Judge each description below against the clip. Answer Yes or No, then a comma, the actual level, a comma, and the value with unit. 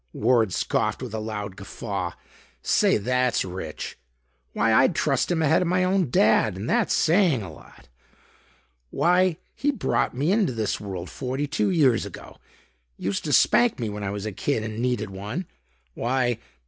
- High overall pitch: No, low, 120 Hz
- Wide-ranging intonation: Yes, wide, 7.4 semitones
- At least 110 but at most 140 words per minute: No, average, 170 wpm